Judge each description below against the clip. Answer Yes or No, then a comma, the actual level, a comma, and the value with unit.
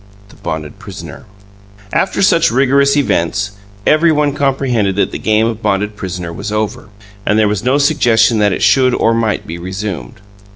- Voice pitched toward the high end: No, low, 110 Hz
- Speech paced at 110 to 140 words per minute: No, average, 170 wpm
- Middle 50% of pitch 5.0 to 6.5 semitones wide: Yes, wide, 5.4 semitones